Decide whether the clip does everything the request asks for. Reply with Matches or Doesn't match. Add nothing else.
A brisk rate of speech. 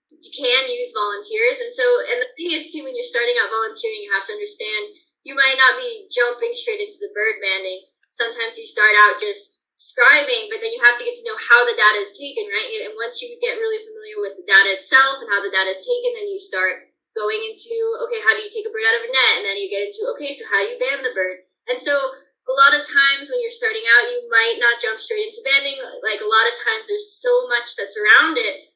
Matches